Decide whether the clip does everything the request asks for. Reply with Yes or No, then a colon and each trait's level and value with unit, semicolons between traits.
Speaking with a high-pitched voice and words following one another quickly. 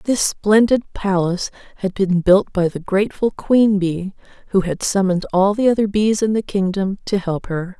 No: high, 195 Hz; average, 185 wpm